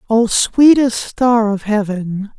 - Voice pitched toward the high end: Yes, high, 220 Hz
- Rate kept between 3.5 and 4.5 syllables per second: No, 3.3 syllables/s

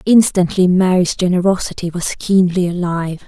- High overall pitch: No, medium, 180 Hz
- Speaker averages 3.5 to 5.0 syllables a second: No, 5.2 syllables/s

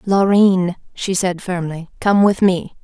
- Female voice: Yes, female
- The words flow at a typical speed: Yes, average, 150 wpm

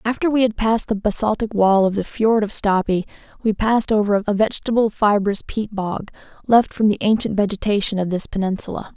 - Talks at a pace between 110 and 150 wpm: No, average, 190 wpm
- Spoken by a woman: Yes, female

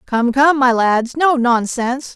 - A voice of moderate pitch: No, very high, 255 Hz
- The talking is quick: No, average, 165 wpm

